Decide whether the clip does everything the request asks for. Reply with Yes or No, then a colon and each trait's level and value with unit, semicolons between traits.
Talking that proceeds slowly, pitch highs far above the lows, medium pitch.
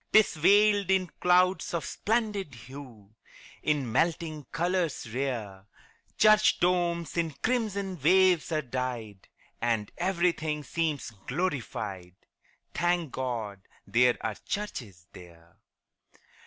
Yes: slow, 100 wpm; wide, 7.3 semitones; medium, 155 Hz